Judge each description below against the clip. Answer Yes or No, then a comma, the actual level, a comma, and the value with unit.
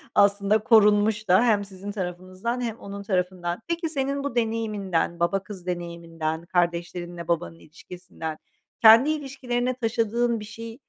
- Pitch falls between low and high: No, high, 205 Hz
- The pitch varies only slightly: No, average, 4.6 semitones